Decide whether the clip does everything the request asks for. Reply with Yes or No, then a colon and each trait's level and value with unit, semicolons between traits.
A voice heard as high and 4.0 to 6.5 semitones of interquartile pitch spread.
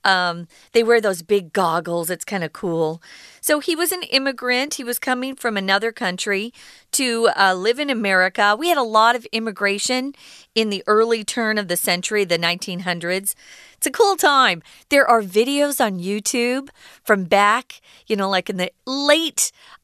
Yes: high, 220 Hz; average, 5.1 semitones